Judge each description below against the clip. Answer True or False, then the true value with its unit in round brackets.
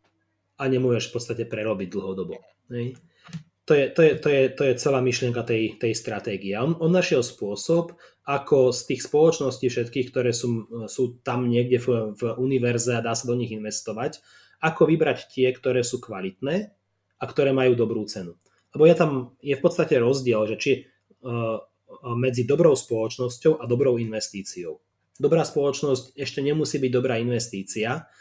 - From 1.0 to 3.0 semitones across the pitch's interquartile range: False (3.5 semitones)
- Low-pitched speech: True (125 Hz)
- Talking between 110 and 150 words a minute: False (160 wpm)